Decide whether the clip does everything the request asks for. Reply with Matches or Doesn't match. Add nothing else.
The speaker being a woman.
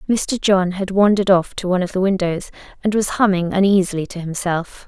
Matches